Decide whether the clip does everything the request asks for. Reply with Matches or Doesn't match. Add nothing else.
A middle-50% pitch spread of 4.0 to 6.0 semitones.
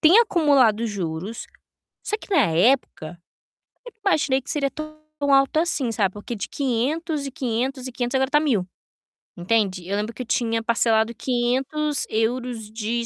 Matches